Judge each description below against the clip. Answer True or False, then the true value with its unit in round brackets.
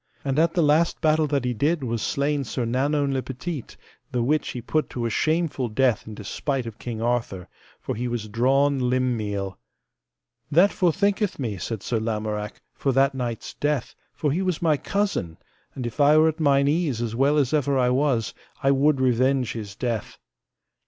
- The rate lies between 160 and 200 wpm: True (190 wpm)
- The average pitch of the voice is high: False (135 Hz)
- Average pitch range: True (4.2 semitones)